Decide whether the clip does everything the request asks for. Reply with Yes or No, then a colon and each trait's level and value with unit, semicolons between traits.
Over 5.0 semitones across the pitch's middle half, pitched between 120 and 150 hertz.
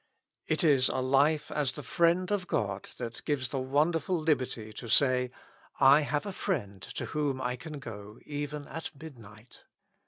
No: average, 3.7 semitones; medium, 140 Hz